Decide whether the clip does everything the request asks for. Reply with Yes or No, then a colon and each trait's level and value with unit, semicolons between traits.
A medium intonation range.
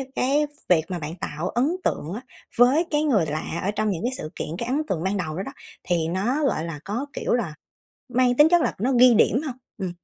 No: wide, 6.8 semitones